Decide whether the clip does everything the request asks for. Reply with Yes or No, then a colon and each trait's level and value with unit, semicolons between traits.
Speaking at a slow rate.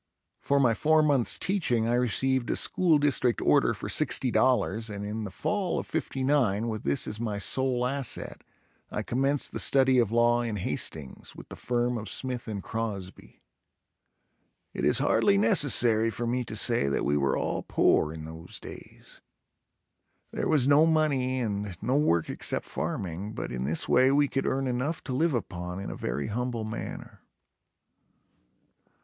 No: average, 165 wpm